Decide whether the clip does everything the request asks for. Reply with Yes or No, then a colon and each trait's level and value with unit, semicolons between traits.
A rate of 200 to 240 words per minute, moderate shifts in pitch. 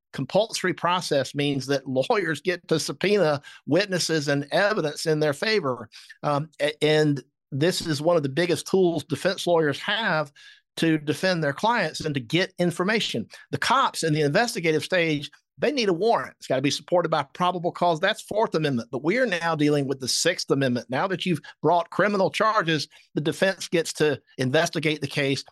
No: average, 180 wpm; average, 3.7 semitones